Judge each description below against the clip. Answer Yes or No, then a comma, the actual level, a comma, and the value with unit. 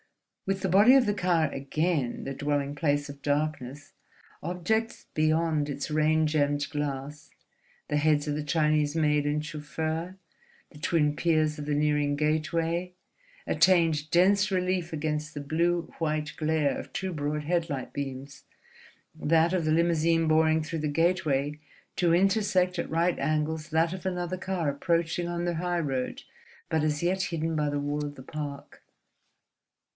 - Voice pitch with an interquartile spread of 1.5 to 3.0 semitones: Yes, average, 2.7 semitones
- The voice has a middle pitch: Yes, medium, 155 Hz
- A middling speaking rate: Yes, average, 150 wpm